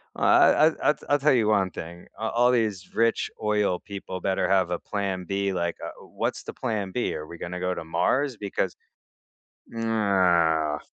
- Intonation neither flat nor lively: Yes, average, 4.0 semitones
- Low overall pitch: Yes, low, 100 Hz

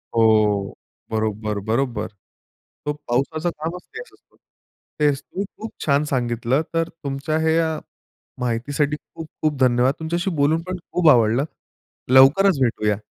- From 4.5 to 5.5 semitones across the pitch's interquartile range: Yes, average, 5.2 semitones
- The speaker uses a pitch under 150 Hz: Yes, medium, 140 Hz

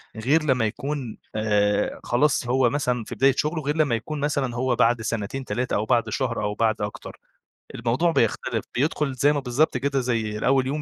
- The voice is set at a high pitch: No, low, 125 Hz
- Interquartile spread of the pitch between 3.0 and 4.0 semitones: Yes, average, 3.5 semitones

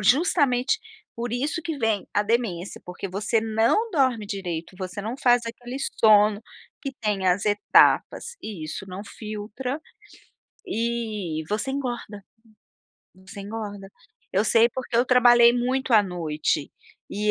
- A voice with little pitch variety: No, average, 3.6 semitones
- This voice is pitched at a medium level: No, high, 220 Hz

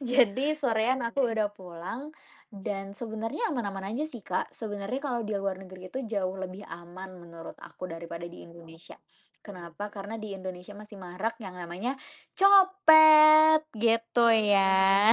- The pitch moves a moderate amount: Yes, average, 4.3 semitones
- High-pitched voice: Yes, high, 205 Hz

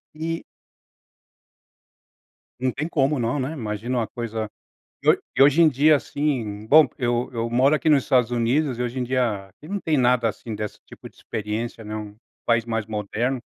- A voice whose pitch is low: Yes, low, 120 Hz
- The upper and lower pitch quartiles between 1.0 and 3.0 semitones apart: No, average, 4.0 semitones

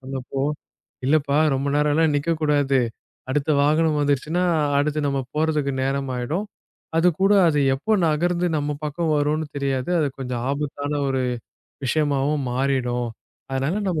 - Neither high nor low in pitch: Yes, medium, 145 Hz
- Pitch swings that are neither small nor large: No, narrow, 2.3 semitones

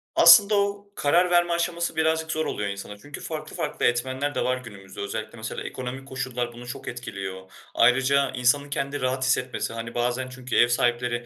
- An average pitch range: Yes, average, 3.3 semitones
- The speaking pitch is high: No, low, 130 Hz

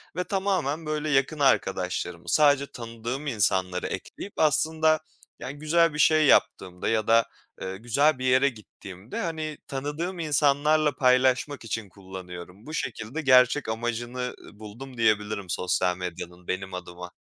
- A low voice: Yes, low, 125 Hz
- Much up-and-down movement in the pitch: Yes, wide, 7.2 semitones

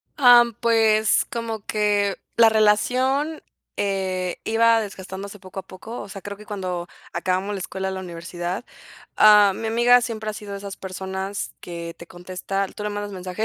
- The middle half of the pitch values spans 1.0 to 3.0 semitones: Yes, average, 2.7 semitones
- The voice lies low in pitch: No, high, 205 Hz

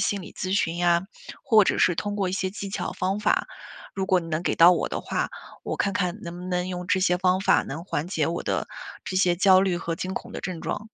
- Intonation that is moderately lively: No, narrow, 1.8 semitones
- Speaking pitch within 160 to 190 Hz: Yes, medium, 185 Hz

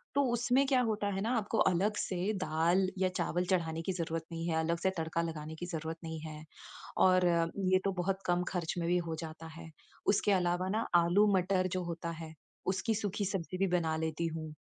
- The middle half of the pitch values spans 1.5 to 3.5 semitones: Yes, average, 2.8 semitones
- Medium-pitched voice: Yes, medium, 175 Hz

